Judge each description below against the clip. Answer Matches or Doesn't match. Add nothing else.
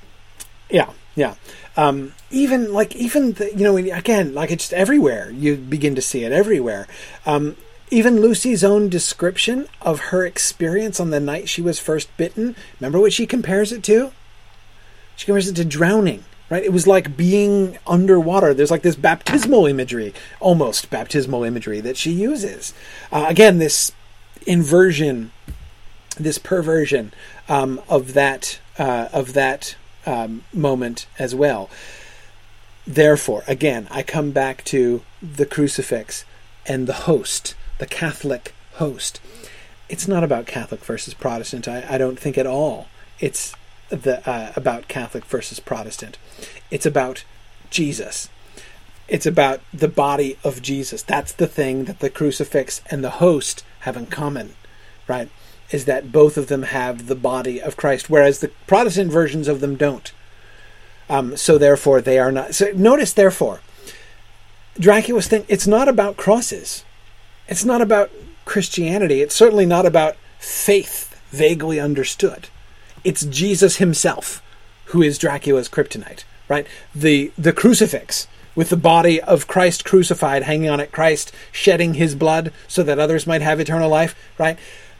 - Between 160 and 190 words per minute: Doesn't match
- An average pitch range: Doesn't match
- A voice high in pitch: Doesn't match